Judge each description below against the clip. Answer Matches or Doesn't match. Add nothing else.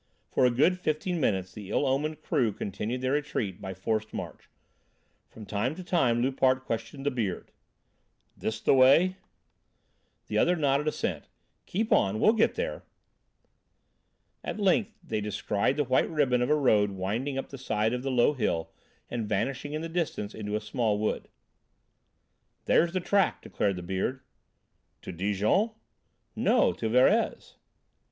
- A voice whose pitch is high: Doesn't match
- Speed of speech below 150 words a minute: Doesn't match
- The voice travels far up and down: Matches